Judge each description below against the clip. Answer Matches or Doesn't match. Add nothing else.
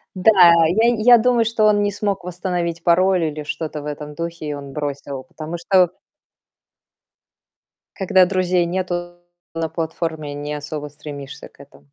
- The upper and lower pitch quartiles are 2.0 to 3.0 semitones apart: Doesn't match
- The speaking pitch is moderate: Matches